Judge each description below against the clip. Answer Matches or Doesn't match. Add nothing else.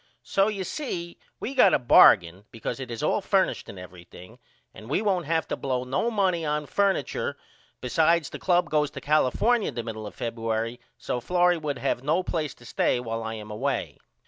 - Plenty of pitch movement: Matches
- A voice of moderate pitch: Matches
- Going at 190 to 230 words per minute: Matches